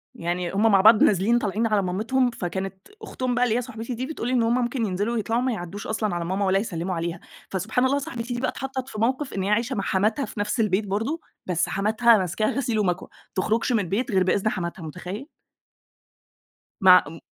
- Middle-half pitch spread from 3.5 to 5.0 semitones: Yes, average, 4.2 semitones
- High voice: Yes, high, 215 Hz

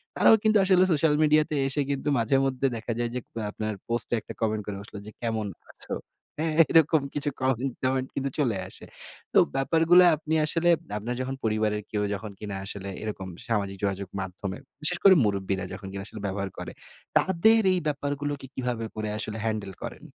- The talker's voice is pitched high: No, low, 120 Hz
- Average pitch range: No, wide, 5.9 semitones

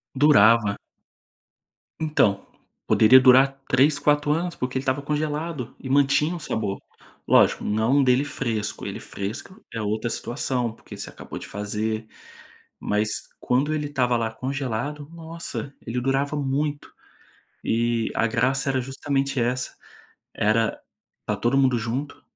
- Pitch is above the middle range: No, low, 130 Hz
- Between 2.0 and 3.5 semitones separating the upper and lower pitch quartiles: No, average, 3.9 semitones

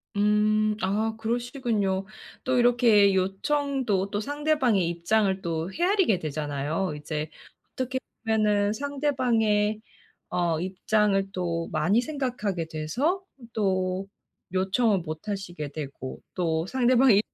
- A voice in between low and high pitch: No, high, 205 Hz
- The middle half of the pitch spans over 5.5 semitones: No, average, 5.2 semitones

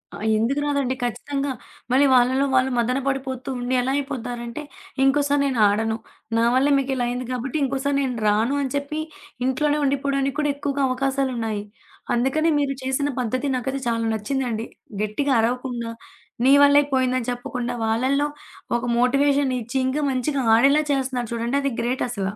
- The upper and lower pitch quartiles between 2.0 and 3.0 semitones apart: Yes, narrow, 2.4 semitones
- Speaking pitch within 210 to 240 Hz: No, very high, 260 Hz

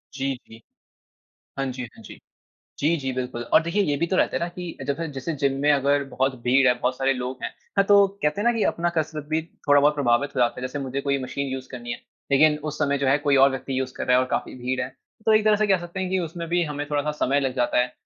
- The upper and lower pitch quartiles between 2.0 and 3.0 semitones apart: No, average, 3.7 semitones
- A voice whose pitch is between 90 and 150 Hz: Yes, medium, 140 Hz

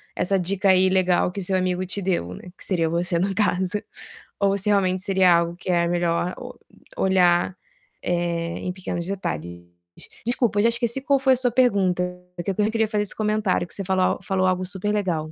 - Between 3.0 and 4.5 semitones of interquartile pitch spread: No, narrow, 2.6 semitones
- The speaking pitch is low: No, medium, 185 Hz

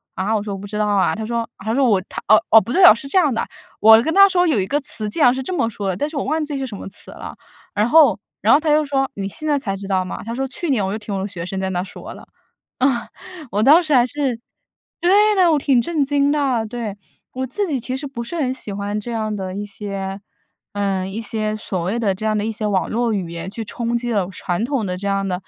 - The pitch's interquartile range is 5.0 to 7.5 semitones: Yes, wide, 5.5 semitones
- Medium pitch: No, high, 225 Hz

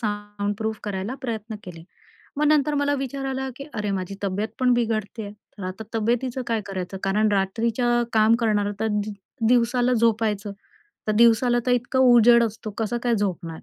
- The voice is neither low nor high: No, high, 220 Hz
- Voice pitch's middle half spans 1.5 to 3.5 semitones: Yes, average, 2.8 semitones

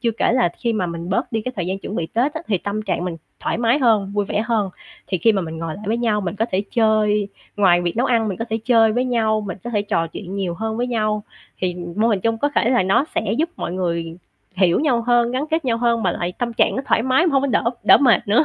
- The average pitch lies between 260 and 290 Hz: No, high, 220 Hz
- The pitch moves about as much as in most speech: Yes, average, 3.9 semitones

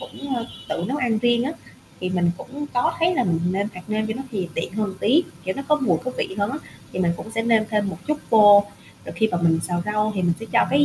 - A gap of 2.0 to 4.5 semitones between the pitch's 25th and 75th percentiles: No, average, 5.1 semitones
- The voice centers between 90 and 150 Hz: No, high, 215 Hz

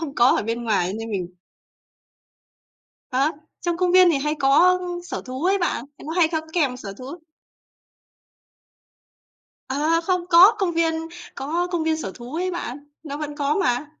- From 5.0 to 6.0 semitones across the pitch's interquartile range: Yes, average, 5.3 semitones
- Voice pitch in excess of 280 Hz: Yes, very high, 305 Hz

